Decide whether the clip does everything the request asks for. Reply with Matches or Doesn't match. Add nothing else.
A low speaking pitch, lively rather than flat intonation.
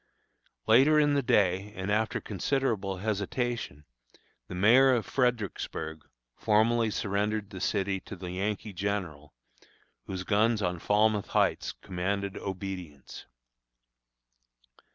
Doesn't match